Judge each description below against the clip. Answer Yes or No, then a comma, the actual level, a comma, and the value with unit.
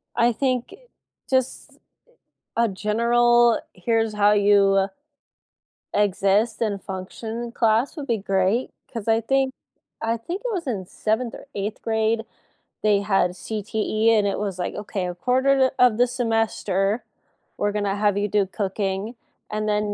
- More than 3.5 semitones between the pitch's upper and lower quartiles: No, average, 2.7 semitones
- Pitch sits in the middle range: No, high, 215 Hz